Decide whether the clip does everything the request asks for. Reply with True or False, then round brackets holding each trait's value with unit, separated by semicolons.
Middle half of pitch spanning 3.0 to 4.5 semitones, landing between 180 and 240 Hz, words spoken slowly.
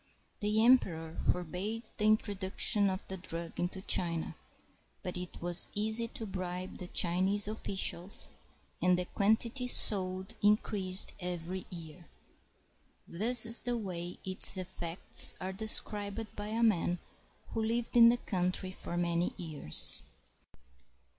True (3.4 semitones; 190 Hz; 125 wpm)